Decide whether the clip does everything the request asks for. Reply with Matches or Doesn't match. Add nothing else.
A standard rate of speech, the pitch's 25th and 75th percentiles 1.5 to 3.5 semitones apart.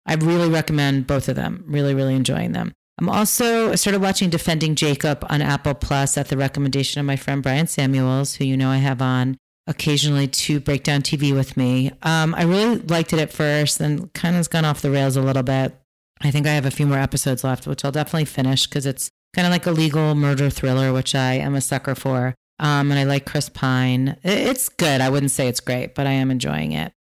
Doesn't match